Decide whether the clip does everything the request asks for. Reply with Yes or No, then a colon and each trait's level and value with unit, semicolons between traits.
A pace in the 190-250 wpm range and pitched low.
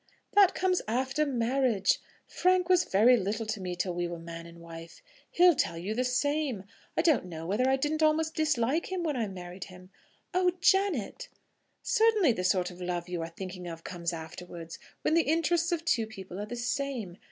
No: average, 195 wpm; high, 230 Hz